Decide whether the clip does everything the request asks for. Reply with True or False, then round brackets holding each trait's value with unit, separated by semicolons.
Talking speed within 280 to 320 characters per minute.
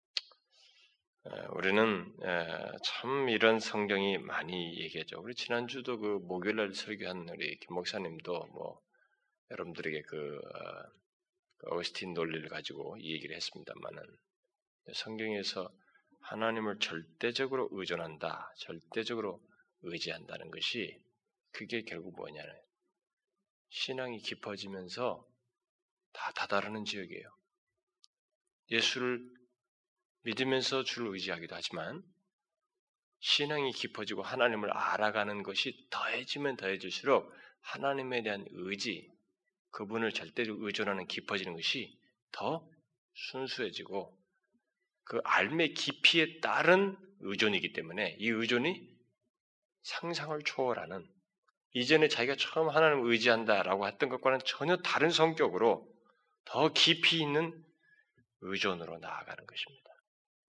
False (265 characters per minute)